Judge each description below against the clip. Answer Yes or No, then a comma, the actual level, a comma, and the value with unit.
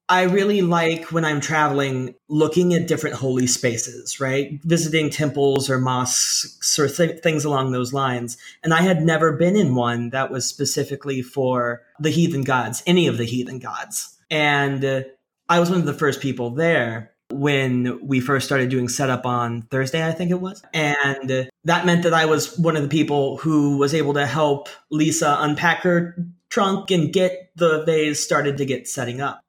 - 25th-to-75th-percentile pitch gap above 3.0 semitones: Yes, average, 3.9 semitones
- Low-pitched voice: No, medium, 145 Hz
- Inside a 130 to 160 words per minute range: No, average, 185 wpm